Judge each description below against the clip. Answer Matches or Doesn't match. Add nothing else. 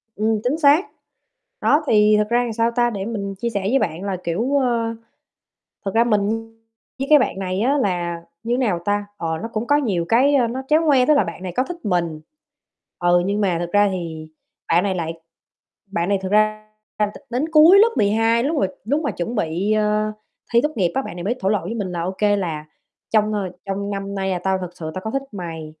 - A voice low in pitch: Doesn't match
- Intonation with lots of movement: Doesn't match